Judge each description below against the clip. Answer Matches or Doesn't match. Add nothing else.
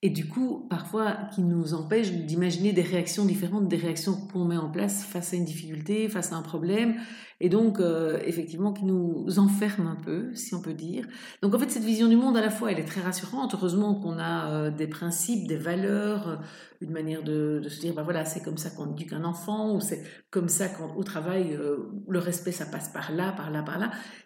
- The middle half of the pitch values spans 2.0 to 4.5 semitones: Matches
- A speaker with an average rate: Doesn't match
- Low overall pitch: Doesn't match